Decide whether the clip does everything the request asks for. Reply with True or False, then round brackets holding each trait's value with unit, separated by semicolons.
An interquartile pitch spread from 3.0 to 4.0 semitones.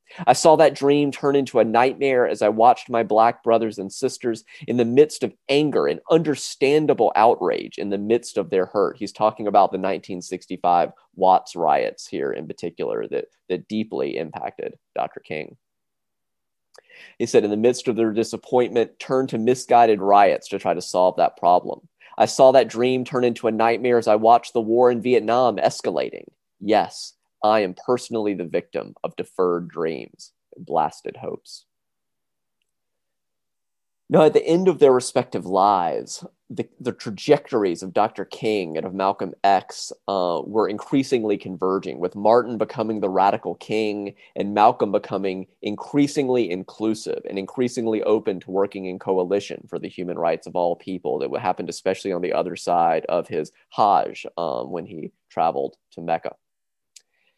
False (4.7 semitones)